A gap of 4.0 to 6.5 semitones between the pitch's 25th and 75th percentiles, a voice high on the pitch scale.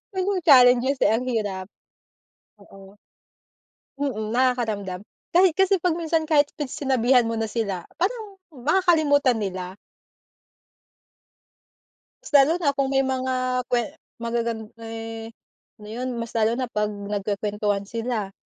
Yes: average, 5.3 semitones; high, 240 Hz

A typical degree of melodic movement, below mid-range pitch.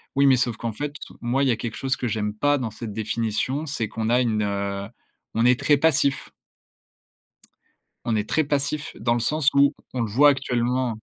Yes: average, 3.9 semitones; low, 125 Hz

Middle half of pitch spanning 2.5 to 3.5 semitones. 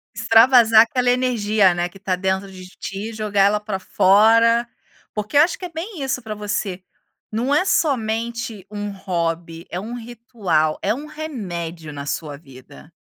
No: average, 4.3 semitones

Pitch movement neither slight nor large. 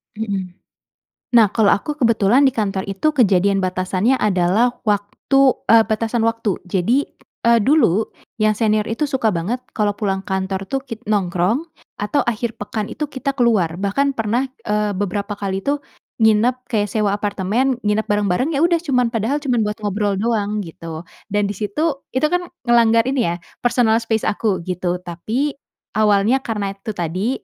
Yes: average, 3.5 semitones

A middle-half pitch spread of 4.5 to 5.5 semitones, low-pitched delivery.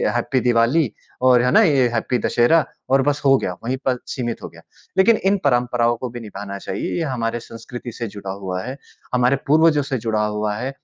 No: average, 3.0 semitones; low, 120 Hz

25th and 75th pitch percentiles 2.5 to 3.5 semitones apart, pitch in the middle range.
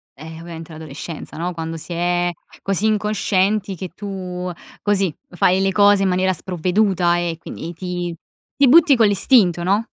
Yes: average, 2.8 semitones; medium, 180 Hz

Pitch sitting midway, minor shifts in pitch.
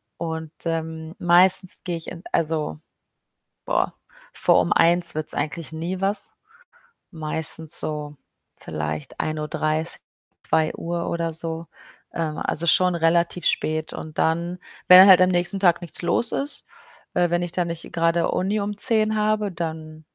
Yes: medium, 170 Hz; narrow, 2.2 semitones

